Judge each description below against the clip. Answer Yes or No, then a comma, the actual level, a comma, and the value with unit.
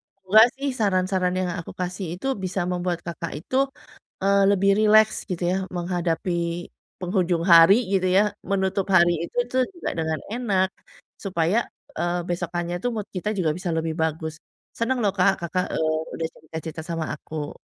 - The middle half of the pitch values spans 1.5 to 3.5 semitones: Yes, average, 2.7 semitones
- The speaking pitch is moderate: Yes, medium, 180 Hz